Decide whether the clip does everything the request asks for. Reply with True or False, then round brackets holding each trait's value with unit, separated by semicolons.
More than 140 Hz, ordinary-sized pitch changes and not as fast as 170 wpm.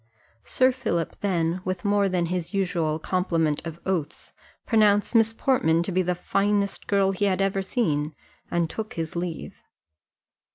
True (185 Hz; 3.3 semitones; 155 wpm)